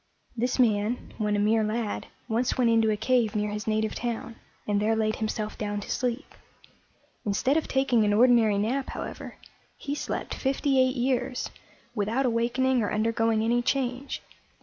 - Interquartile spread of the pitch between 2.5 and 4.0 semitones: Yes, average, 2.9 semitones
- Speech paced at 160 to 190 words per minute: Yes, average, 165 wpm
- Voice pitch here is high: Yes, high, 230 Hz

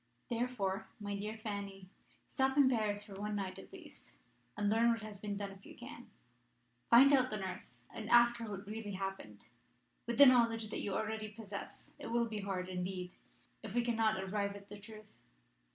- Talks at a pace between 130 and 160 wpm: No, average, 190 wpm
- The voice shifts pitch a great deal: No, average, 2.7 semitones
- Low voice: No, high, 210 Hz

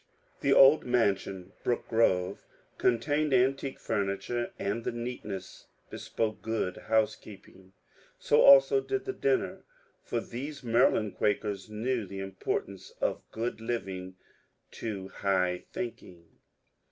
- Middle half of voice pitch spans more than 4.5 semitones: Yes, average, 4.9 semitones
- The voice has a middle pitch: No, low, 115 Hz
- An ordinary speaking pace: No, slow, 120 wpm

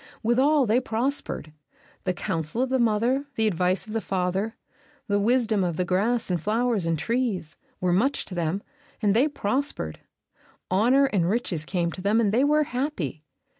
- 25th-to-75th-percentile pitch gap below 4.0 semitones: No, average, 5.3 semitones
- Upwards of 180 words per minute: No, average, 170 wpm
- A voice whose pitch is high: Yes, high, 215 Hz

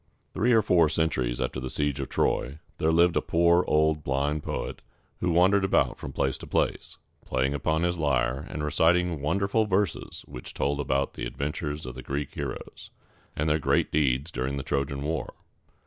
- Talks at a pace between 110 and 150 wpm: No, average, 180 wpm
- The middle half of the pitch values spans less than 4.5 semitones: Yes, average, 3.8 semitones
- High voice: No, very low, 75 Hz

